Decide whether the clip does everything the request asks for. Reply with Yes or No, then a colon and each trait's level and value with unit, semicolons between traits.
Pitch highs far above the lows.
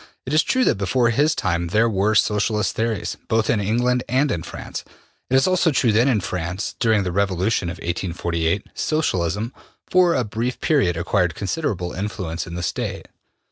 Yes: wide, 5.8 semitones